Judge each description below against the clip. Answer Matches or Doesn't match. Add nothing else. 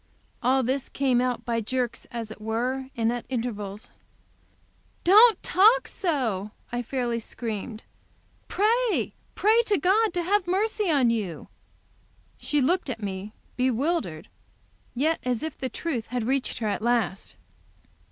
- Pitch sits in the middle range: Doesn't match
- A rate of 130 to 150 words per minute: Matches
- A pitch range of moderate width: Doesn't match